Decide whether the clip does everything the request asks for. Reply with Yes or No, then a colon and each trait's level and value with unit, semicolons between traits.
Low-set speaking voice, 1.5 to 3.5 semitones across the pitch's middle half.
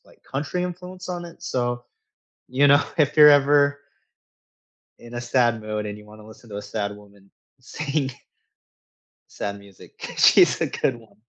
No: low, 120 Hz; wide, 5.4 semitones